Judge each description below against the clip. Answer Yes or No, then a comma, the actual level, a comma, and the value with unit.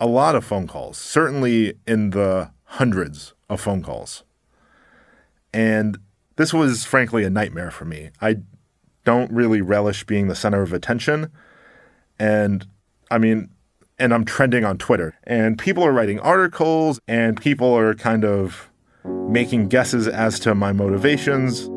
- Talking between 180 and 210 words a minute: No, average, 145 wpm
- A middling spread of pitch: Yes, average, 3.7 semitones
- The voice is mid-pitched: No, low, 110 Hz